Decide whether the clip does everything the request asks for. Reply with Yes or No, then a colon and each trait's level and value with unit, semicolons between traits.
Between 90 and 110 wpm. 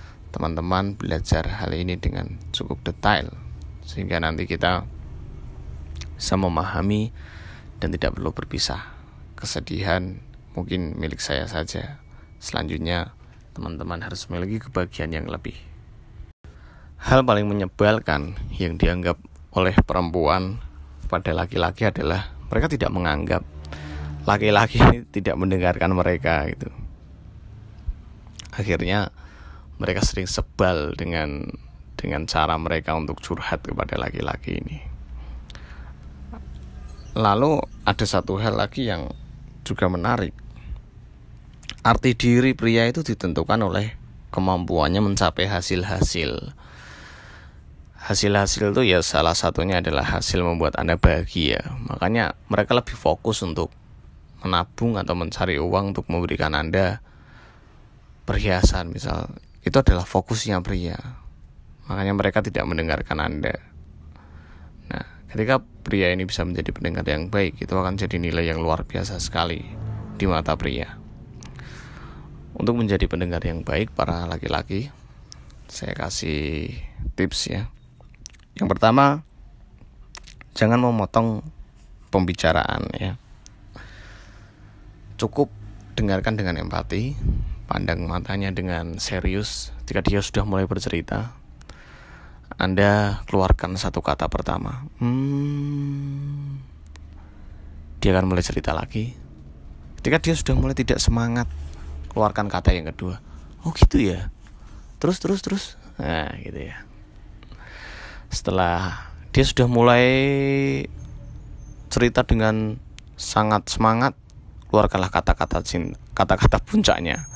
Yes: average, 105 wpm